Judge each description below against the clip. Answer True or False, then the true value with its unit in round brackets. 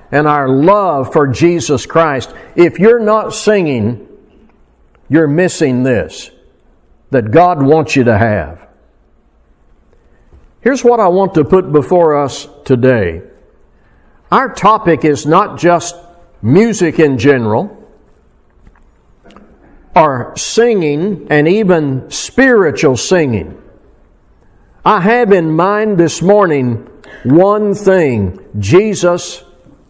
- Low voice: False (160 Hz)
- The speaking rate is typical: False (100 wpm)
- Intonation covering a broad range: True (6.8 semitones)